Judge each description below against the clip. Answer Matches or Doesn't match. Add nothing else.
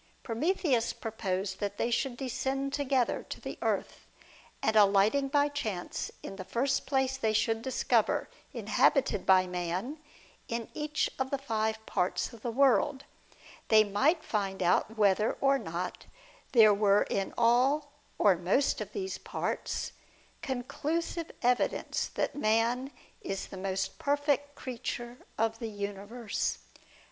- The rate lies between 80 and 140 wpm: Matches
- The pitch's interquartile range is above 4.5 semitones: Matches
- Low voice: Doesn't match